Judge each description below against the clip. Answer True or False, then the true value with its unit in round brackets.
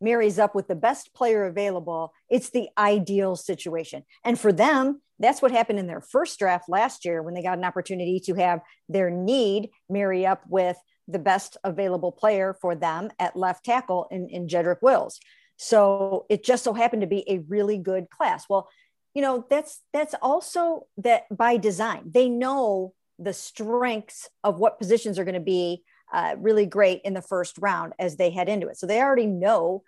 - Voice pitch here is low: False (200 Hz)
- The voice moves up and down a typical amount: True (4.2 semitones)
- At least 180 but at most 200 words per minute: True (190 wpm)